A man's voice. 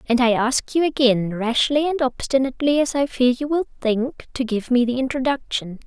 No: female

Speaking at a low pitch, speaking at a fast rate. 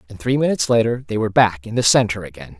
Yes: low, 110 Hz; fast, 255 wpm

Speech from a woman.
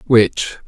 No: male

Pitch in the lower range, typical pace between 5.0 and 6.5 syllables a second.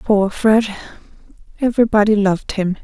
No: high, 210 Hz; 5.7 syllables/s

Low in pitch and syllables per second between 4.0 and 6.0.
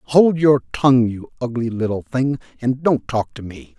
Yes: low, 120 Hz; 4.7 syllables/s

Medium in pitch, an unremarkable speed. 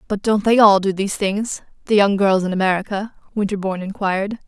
No: high, 200 Hz; average, 175 wpm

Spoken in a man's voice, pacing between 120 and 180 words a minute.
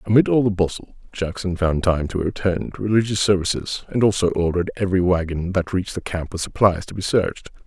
No: male; average, 195 wpm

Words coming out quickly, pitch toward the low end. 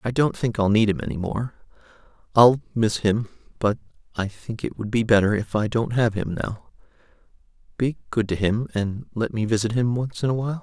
Yes: fast, 210 wpm; low, 110 Hz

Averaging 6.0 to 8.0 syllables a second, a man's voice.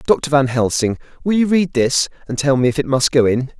No: 5.4 syllables/s; male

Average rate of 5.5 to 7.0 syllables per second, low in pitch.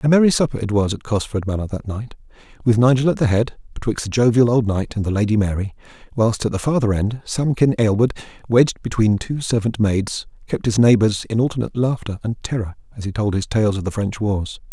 Yes: 5.8 syllables/s; low, 110 Hz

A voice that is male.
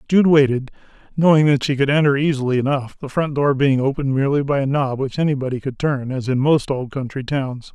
Yes: male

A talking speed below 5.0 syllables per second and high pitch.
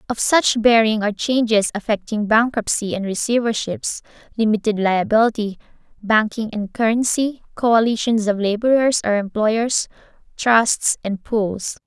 Yes: 4.6 syllables/s; high, 220 Hz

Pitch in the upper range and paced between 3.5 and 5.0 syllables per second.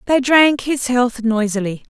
Yes: high, 245 Hz; 4.1 syllables/s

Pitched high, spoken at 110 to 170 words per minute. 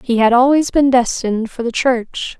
No: very high, 250 Hz; average, 200 wpm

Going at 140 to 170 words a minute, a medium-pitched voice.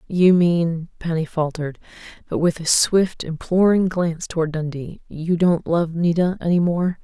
Yes: average, 155 wpm; medium, 170 Hz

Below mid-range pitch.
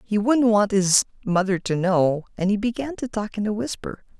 No: high, 205 Hz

